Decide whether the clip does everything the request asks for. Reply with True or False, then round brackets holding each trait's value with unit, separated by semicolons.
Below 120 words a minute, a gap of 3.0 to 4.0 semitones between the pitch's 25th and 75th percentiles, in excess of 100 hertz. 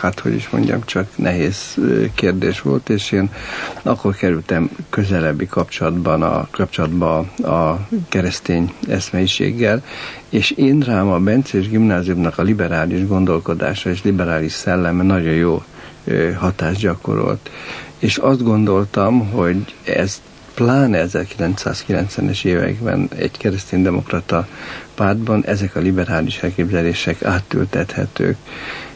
False (105 wpm; 3.5 semitones; 95 Hz)